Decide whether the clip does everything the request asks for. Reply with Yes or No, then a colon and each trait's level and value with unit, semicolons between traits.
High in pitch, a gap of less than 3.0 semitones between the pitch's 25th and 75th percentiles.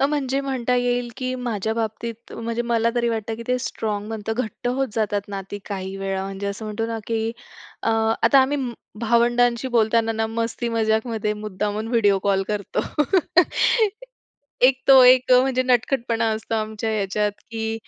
Yes: high, 225 Hz; narrow, 2.4 semitones